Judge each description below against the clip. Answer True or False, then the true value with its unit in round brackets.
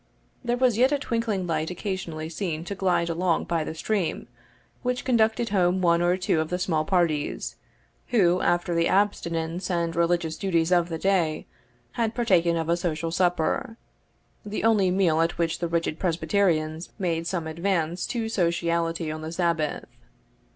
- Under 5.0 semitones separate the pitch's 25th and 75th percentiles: True (2.9 semitones)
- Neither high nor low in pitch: True (175 Hz)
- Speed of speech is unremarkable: True (165 wpm)